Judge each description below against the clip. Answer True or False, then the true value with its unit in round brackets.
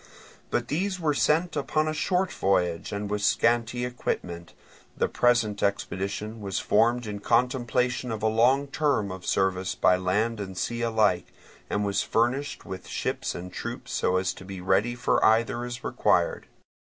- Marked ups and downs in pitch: False (4.2 semitones)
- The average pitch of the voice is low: True (110 Hz)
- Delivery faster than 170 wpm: False (165 wpm)